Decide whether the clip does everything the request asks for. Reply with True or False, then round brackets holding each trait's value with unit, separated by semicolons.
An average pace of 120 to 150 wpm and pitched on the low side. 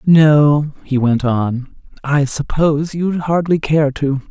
False (140 wpm; 145 Hz)